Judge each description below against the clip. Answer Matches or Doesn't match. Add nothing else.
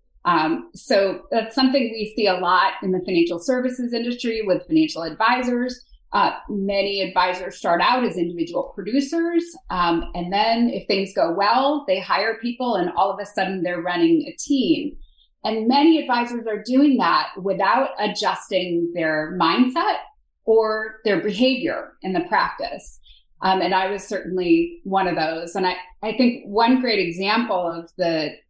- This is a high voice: Matches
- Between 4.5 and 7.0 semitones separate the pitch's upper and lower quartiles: Matches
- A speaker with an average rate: Matches